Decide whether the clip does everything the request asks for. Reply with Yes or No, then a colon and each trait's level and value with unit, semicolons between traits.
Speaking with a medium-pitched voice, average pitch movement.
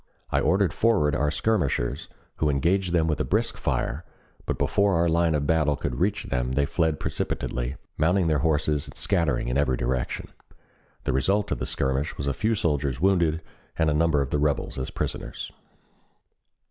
No: very low, 75 Hz; average, 3.5 semitones